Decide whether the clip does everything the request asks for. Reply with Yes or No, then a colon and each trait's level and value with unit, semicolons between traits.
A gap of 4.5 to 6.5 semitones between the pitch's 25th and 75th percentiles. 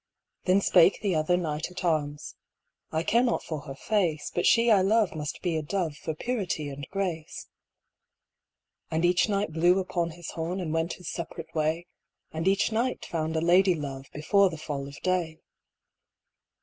No: average, 3.2 semitones